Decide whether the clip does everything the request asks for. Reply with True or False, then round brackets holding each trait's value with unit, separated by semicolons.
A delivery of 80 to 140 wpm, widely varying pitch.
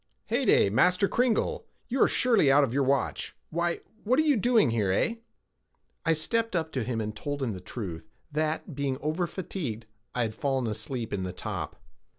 False (185 wpm; 8.1 semitones)